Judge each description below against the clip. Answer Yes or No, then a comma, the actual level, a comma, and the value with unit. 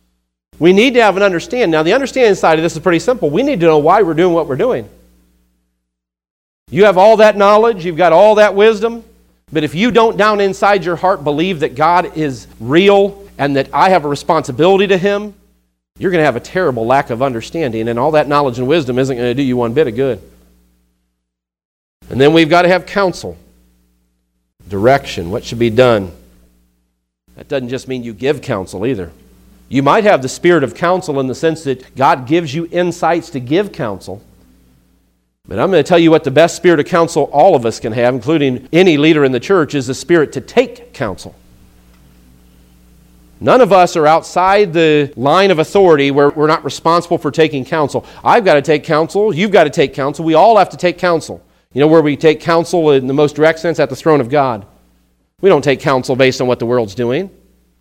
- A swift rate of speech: Yes, fast, 215 wpm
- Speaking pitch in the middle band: Yes, medium, 145 Hz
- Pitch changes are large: Yes, wide, 7.4 semitones